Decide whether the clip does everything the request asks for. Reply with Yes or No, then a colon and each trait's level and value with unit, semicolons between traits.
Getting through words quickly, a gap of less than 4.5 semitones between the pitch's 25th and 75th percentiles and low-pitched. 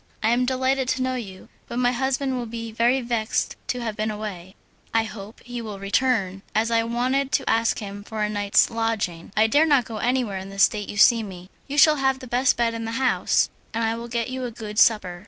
No: fast, 240 wpm; average, 3.1 semitones; high, 230 Hz